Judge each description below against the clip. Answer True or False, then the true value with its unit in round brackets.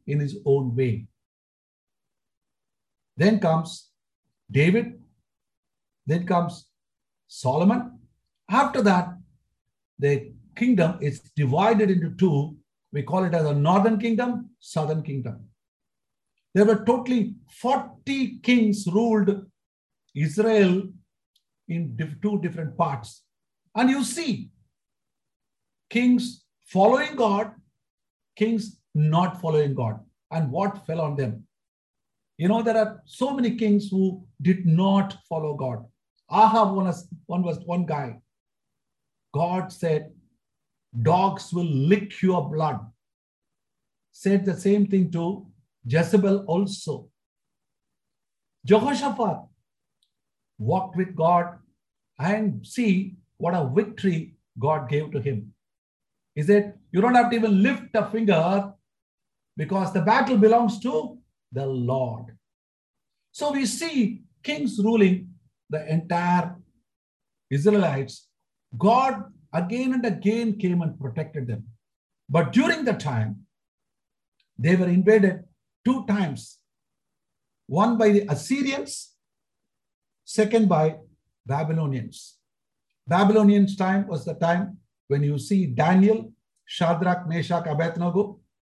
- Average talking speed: False (110 wpm)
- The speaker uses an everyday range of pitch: False (5.8 semitones)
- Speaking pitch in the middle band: True (180 Hz)